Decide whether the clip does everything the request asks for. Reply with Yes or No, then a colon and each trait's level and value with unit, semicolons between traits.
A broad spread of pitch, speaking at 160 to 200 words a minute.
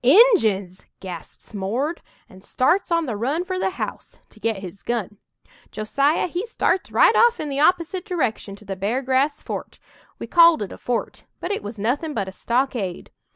Yes: wide, 8.5 semitones; average, 180 wpm